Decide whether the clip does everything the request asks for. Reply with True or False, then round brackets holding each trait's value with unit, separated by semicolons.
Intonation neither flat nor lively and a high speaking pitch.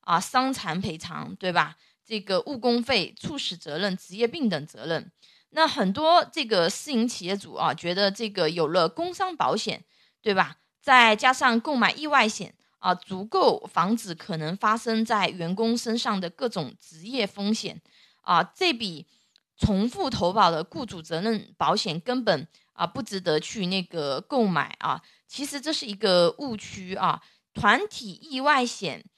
False (5.9 semitones; 210 Hz)